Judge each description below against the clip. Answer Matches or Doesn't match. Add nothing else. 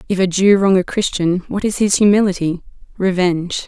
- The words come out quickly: Doesn't match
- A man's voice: Doesn't match